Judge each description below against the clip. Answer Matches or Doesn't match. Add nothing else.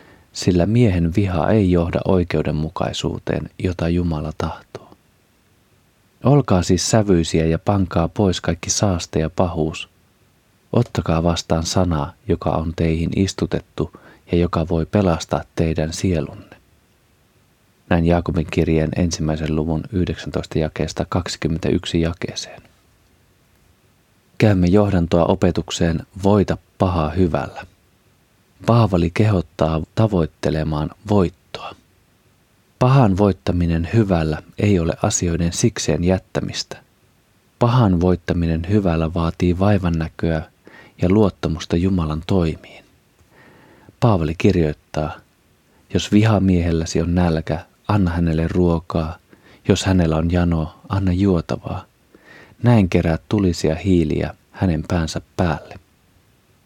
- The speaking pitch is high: Doesn't match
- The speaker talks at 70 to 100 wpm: Matches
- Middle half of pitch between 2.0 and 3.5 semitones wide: Matches